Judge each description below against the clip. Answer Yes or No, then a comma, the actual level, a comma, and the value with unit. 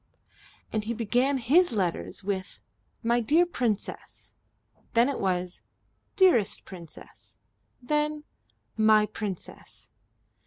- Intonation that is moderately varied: No, wide, 6.0 semitones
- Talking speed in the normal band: No, slow, 95 wpm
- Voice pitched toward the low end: No, high, 225 Hz